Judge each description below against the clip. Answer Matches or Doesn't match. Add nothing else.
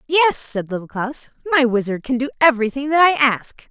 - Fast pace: Doesn't match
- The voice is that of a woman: Matches